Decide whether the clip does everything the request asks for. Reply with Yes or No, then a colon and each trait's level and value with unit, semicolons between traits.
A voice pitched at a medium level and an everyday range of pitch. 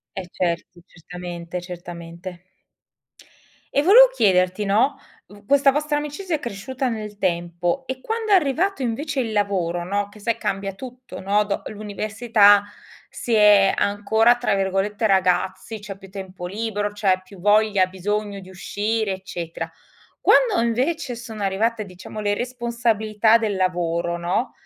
No: high, 205 Hz; average, 4.0 semitones